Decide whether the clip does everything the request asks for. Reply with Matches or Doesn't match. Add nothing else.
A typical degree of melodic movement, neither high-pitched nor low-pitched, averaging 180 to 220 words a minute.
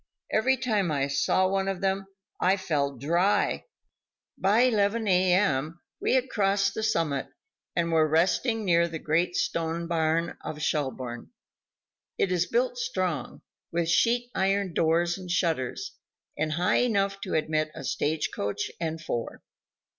Doesn't match